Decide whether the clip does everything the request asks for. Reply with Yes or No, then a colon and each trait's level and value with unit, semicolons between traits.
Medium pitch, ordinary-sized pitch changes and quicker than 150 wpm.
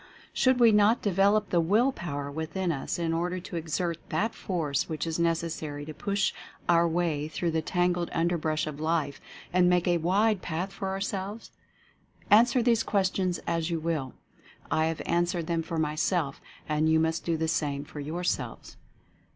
Yes: medium, 170 Hz; average, 3.1 semitones; average, 175 wpm